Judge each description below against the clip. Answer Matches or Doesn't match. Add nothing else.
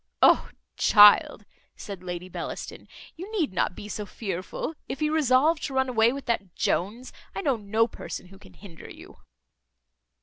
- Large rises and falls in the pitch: Matches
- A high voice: Matches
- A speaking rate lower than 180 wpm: Matches